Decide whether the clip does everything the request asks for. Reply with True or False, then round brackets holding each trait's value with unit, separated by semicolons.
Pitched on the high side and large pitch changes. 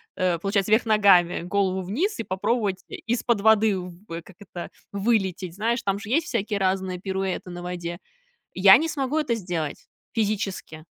False (195 Hz; 3.3 semitones)